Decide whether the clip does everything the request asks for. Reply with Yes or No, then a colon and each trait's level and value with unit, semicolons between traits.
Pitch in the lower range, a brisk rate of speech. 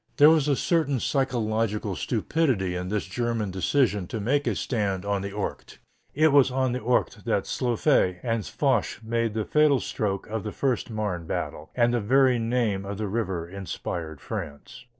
No: low, 110 Hz; average, 175 wpm